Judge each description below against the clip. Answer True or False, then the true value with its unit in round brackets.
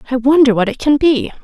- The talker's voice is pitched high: True (265 Hz)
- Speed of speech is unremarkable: False (250 wpm)